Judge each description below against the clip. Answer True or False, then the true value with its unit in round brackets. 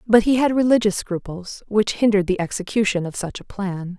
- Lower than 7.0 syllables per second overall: True (5.5 syllables/s)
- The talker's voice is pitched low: False (200 Hz)